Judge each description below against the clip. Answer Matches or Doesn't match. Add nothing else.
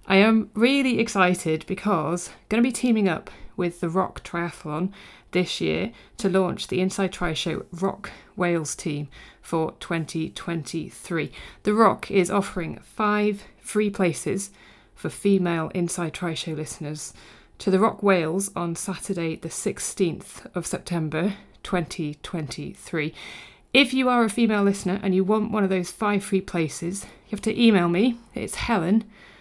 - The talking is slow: Doesn't match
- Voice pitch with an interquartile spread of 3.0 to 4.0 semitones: Matches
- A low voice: Doesn't match